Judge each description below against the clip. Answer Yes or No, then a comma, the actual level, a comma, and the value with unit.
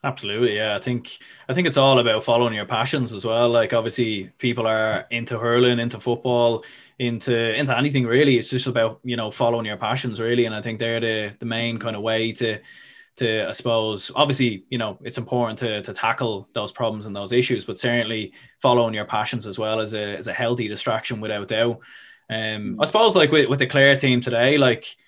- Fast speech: Yes, fast, 210 wpm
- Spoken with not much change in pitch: Yes, narrow, 2.0 semitones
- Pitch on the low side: Yes, low, 115 Hz